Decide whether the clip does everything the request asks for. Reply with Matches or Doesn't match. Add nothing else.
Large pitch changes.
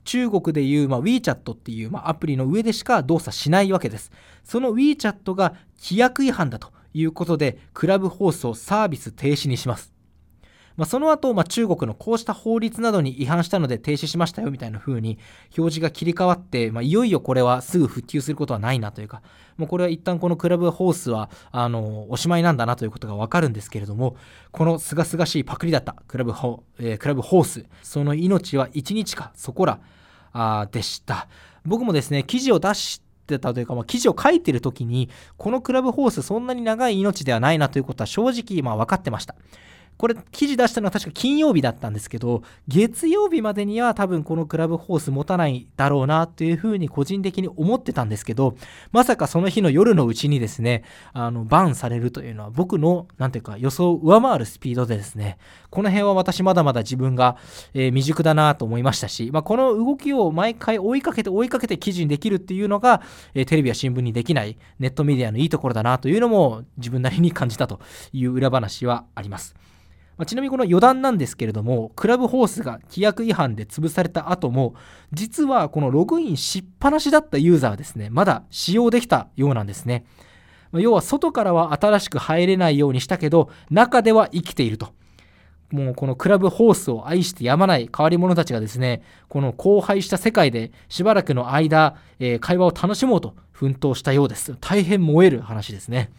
Matches